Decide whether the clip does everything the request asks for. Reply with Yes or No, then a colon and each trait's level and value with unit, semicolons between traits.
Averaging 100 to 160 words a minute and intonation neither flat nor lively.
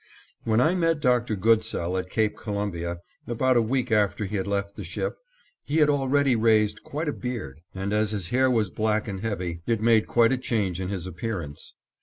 No: average, 200 wpm; average, 4.2 semitones